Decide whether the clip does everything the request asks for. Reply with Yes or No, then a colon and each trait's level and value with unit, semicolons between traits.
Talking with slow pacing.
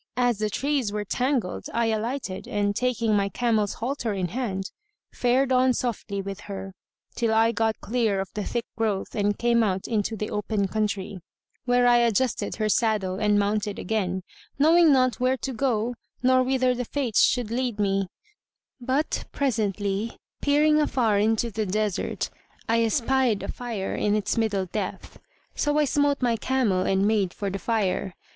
No: average, 165 wpm